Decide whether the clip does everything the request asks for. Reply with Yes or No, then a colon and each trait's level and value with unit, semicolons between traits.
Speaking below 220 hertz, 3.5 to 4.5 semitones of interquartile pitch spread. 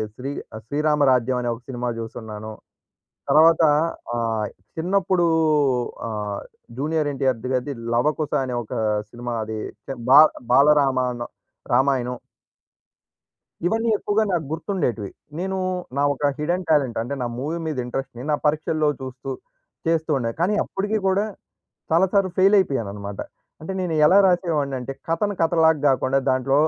No: medium, 140 Hz; average, 5.0 semitones